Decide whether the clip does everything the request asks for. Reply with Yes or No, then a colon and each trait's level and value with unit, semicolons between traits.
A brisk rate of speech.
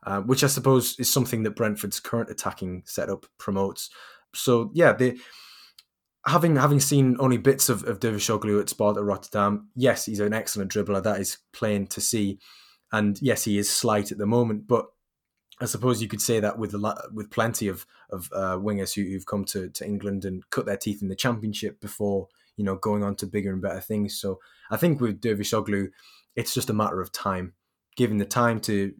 Yes: fast, 210 wpm